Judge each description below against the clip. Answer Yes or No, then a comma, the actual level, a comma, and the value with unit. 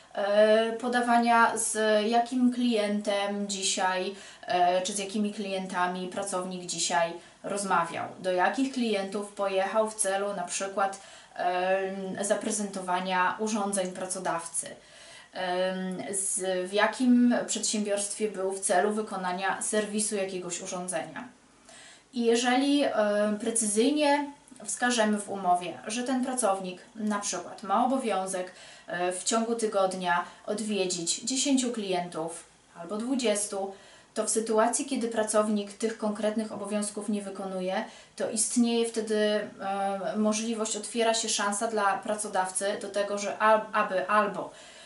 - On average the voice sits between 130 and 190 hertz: No, high, 205 Hz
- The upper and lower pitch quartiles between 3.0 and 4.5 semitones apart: No, narrow, 2.6 semitones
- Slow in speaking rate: Yes, slow, 105 wpm